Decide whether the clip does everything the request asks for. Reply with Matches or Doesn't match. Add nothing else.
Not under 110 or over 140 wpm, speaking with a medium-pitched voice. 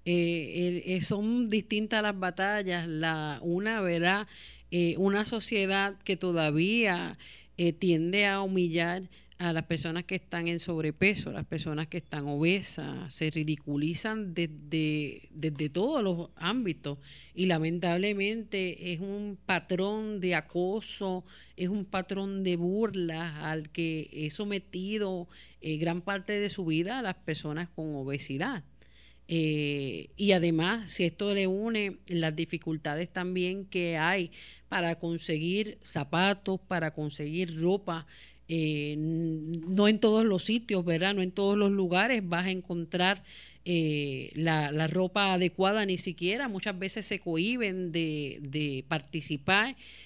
Matches